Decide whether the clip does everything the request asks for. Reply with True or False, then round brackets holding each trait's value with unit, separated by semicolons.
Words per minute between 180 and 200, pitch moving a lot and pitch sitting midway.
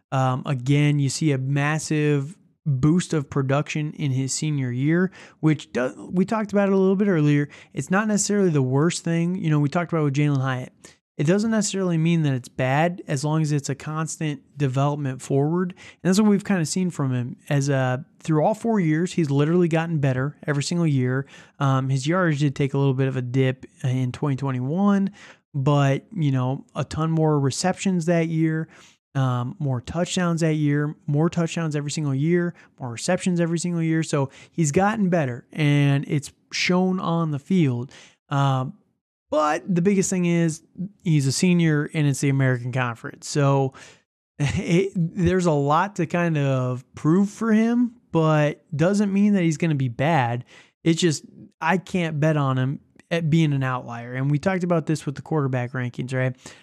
False (185 wpm; 4.1 semitones; 155 Hz)